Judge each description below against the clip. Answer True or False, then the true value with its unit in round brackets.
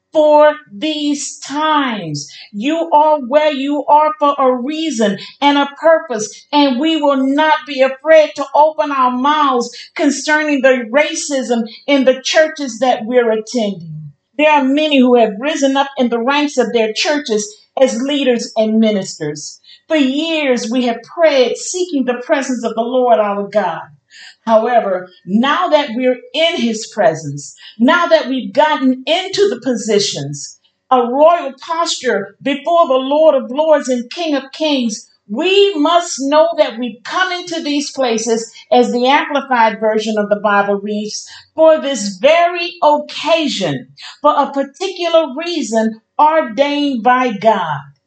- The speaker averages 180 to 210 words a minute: False (145 wpm)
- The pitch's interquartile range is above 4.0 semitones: True (5.1 semitones)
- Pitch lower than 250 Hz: False (270 Hz)